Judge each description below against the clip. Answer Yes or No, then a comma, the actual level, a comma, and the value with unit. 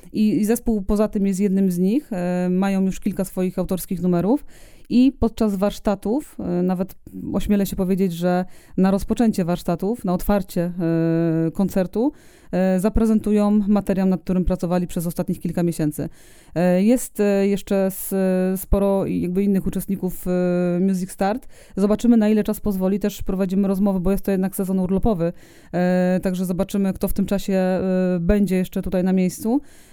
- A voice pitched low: No, high, 195 Hz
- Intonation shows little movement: Yes, narrow, 2.1 semitones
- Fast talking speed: No, average, 140 wpm